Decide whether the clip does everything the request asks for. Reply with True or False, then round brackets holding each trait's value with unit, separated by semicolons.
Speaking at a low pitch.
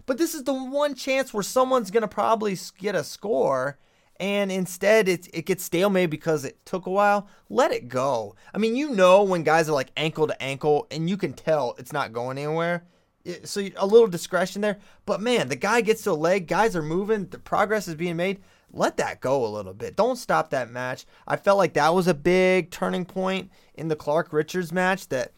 False (185 Hz)